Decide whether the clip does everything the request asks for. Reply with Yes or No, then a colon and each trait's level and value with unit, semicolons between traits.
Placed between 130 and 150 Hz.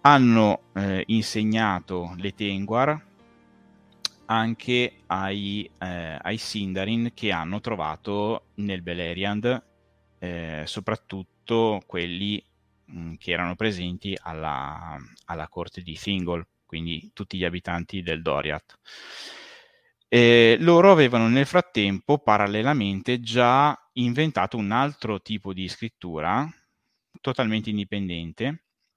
No: low, 100 Hz